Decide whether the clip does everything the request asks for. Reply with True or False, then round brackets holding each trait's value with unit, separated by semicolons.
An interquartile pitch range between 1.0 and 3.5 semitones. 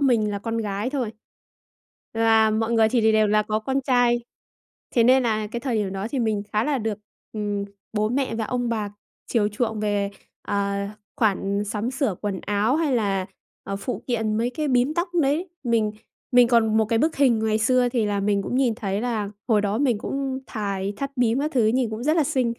True (3.1 semitones)